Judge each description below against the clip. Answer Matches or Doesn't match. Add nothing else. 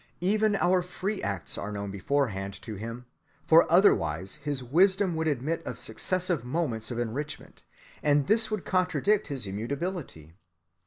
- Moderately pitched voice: Matches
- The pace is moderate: Matches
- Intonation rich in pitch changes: Matches